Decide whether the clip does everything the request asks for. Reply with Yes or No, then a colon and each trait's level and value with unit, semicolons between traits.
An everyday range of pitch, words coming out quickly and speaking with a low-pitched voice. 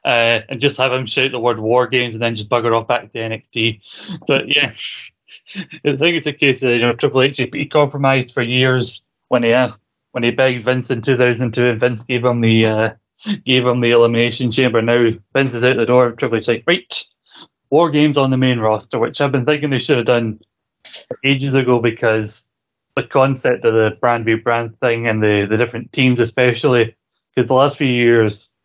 No: narrow, 2.3 semitones; fast, 210 wpm; low, 125 Hz